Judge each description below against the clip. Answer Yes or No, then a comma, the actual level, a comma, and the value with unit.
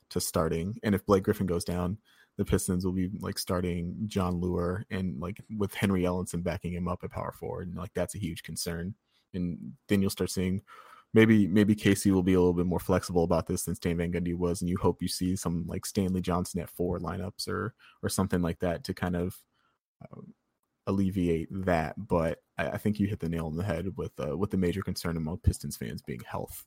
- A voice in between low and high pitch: No, very low, 90 Hz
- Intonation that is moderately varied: No, narrow, 2.1 semitones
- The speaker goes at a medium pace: No, fast, 225 wpm